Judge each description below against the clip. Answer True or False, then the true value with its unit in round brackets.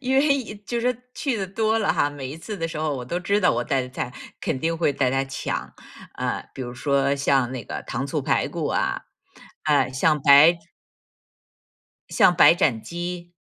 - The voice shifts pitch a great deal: True (5.8 semitones)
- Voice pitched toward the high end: False (150 Hz)